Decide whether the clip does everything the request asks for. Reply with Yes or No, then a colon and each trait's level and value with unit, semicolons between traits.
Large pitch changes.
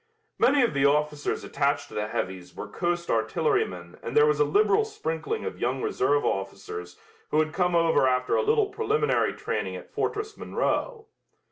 Yes: wide, 8.9 semitones